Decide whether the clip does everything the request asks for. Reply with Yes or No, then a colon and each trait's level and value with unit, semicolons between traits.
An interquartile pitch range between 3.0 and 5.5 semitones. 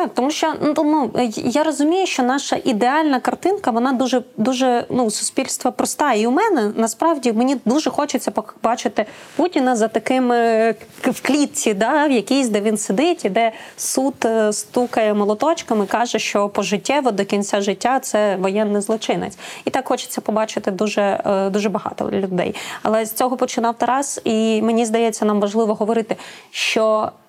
Yes: average, 3.3 semitones